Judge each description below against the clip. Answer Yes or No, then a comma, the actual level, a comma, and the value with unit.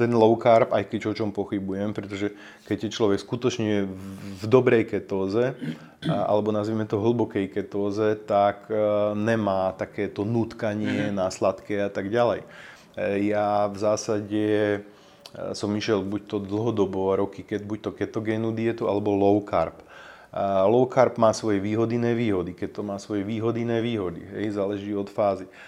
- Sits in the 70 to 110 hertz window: Yes, low, 105 Hz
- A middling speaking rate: Yes, average, 145 wpm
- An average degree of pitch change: No, narrow, 1.7 semitones